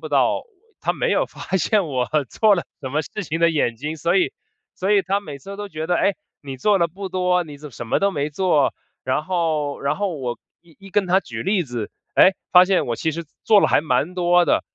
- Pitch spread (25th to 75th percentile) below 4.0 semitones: No, average, 4.6 semitones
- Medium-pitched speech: Yes, medium, 170 Hz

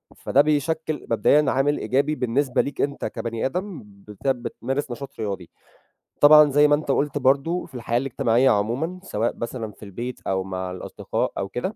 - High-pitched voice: No, low, 135 Hz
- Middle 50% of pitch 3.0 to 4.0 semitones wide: No, average, 4.4 semitones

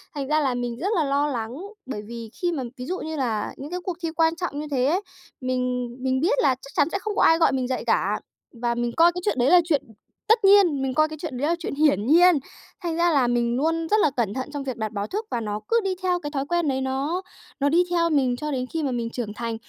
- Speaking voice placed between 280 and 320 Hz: Yes, very high, 285 Hz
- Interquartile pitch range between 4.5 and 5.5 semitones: Yes, average, 5.1 semitones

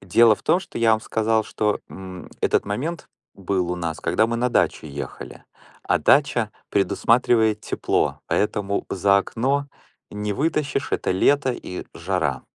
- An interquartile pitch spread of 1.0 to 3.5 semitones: No, average, 4.1 semitones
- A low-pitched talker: Yes, low, 105 Hz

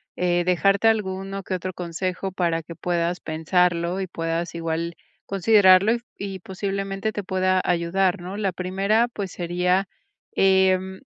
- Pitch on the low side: No, medium, 185 Hz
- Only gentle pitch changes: Yes, narrow, 1.9 semitones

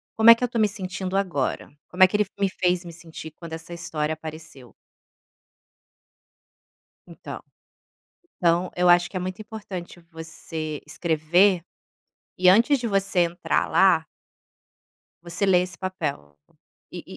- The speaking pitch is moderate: Yes, medium, 180 Hz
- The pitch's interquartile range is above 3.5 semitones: No, average, 3.0 semitones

